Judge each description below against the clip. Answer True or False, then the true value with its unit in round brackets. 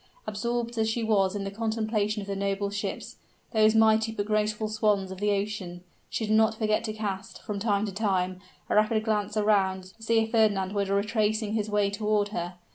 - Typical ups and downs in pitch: False (1.6 semitones)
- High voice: True (210 Hz)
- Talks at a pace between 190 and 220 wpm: True (200 wpm)